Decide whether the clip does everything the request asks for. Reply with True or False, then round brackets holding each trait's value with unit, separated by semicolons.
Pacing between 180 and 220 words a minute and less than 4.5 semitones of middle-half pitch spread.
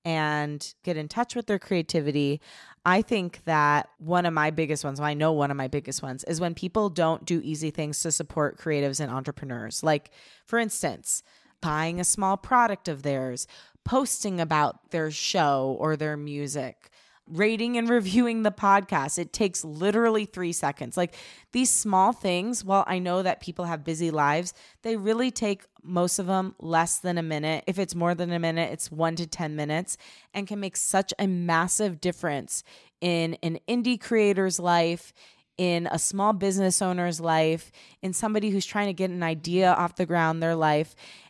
True (185 wpm; 4.1 semitones)